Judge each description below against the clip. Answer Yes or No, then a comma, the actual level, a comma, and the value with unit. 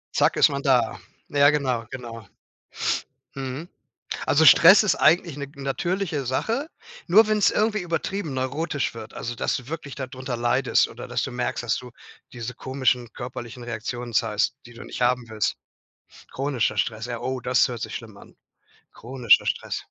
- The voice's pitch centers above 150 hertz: No, low, 130 Hz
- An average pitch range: Yes, average, 3.5 semitones